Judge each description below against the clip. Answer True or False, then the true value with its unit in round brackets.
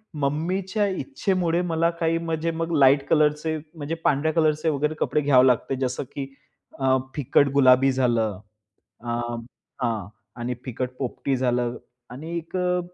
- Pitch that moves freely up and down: False (4.2 semitones)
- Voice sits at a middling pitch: True (145 Hz)